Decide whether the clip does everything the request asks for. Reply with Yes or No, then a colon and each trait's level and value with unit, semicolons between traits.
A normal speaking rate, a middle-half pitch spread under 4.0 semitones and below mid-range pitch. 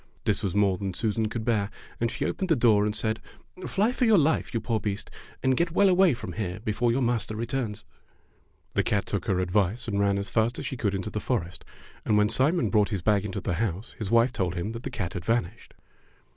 No: fast, 235 wpm; average, 3.3 semitones; low, 110 Hz